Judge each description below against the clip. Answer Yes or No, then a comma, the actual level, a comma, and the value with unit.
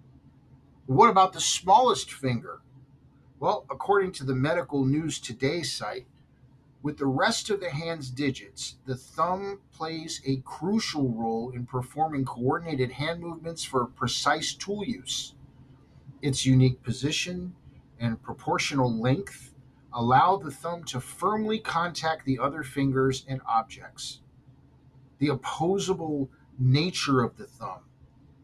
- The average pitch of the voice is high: No, medium, 140 Hz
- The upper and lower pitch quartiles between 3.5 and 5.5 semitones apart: Yes, average, 3.8 semitones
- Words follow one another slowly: Yes, slow, 120 wpm